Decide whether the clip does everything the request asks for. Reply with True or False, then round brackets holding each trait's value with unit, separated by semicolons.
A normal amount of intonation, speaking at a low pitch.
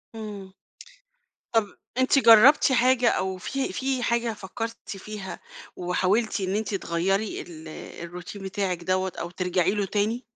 False (3.7 semitones; 205 Hz)